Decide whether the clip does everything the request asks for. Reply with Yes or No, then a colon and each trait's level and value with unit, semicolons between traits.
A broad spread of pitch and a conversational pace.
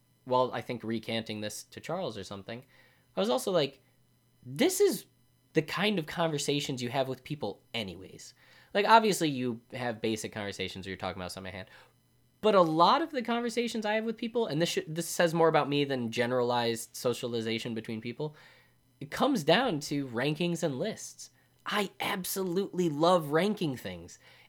Yes: wide, 6.5 semitones; average, 175 wpm